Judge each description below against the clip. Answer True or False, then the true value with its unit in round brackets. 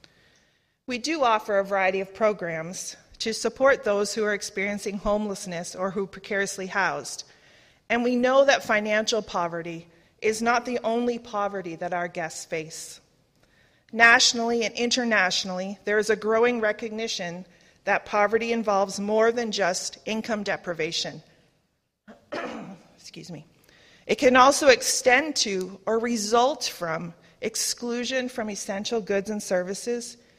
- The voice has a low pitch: False (210 Hz)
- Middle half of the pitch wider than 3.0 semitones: True (3.8 semitones)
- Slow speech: True (130 wpm)